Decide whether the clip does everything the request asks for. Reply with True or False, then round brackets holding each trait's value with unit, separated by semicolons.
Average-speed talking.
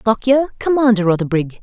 True (185 wpm)